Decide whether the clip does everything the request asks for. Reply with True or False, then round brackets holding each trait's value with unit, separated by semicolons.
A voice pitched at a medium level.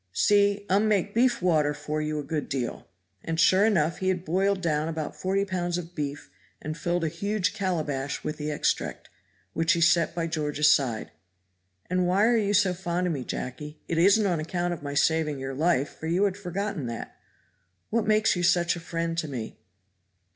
True (170 Hz)